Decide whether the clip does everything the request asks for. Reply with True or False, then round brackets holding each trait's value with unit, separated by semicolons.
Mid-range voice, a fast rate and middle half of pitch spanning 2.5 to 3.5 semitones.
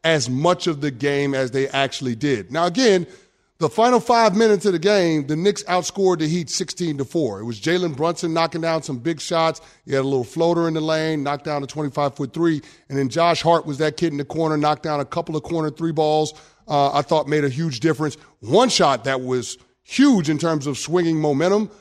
True (160 Hz; 230 wpm; 2.9 semitones)